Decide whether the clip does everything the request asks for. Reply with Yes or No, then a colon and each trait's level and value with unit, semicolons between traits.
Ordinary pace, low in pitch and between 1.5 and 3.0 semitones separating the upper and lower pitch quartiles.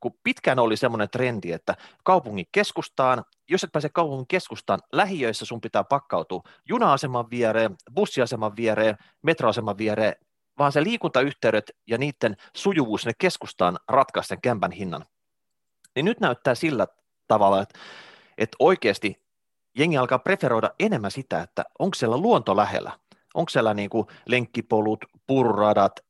No: average, 135 wpm; low, 120 Hz; average, 4.8 semitones